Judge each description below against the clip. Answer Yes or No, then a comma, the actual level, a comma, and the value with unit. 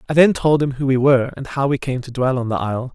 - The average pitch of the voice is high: No, low, 135 Hz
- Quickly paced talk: Yes, fast, 325 wpm